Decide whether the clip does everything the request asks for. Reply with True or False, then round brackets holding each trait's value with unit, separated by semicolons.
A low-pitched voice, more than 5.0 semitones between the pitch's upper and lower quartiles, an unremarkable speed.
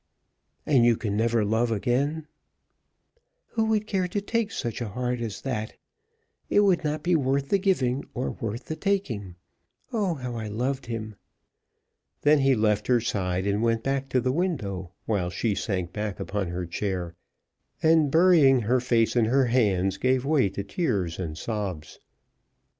True (120 Hz; 5.6 semitones; 160 wpm)